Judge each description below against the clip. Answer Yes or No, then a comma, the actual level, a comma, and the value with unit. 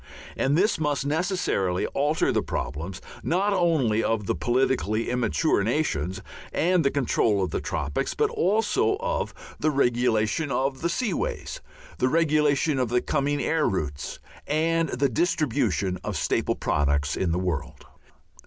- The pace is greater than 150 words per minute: No, average, 145 wpm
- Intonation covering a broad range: Yes, wide, 8.1 semitones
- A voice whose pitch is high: No, low, 135 Hz